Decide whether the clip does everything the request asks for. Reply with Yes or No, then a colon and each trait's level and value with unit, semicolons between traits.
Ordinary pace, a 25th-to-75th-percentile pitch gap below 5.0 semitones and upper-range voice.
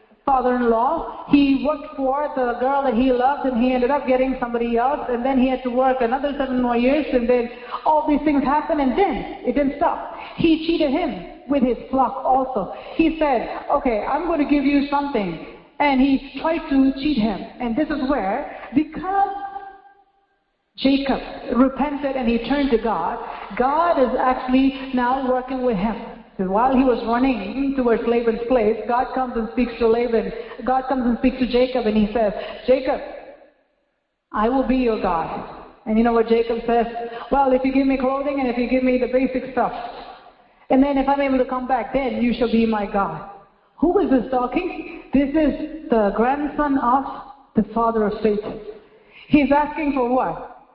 Yes: average, 190 wpm; average, 3.1 semitones; very high, 260 Hz